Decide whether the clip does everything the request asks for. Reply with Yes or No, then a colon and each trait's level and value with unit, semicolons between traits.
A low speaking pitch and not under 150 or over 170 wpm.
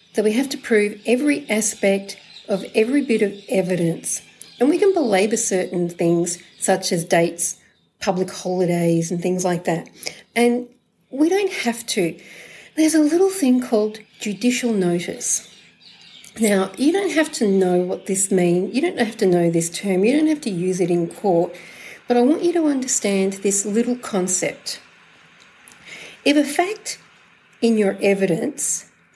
No: high, 205 Hz; average, 165 wpm